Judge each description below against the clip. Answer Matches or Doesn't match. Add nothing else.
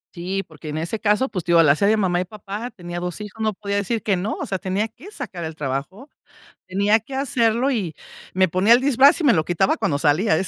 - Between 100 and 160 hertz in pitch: Doesn't match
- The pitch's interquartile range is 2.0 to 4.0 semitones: Doesn't match